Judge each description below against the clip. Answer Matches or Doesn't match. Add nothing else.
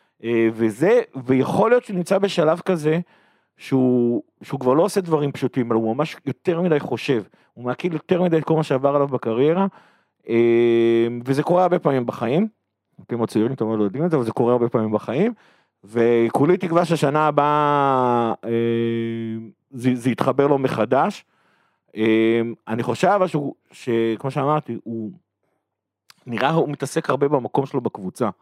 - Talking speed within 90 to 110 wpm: Doesn't match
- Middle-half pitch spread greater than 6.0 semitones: Doesn't match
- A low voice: Matches